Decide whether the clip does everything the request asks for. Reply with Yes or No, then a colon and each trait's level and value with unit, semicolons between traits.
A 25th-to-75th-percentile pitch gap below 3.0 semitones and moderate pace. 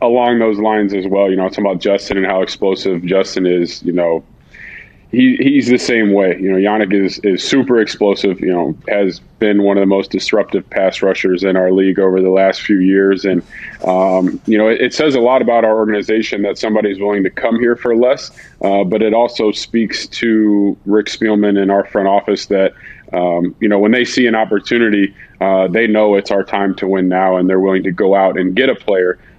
No: narrow, 2.5 semitones; fast, 220 wpm